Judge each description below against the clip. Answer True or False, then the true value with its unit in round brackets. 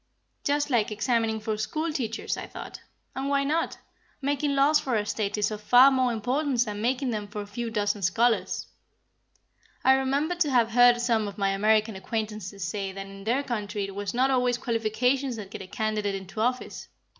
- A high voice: True (225 Hz)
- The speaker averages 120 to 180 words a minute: False (190 wpm)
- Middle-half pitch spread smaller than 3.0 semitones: False (3.9 semitones)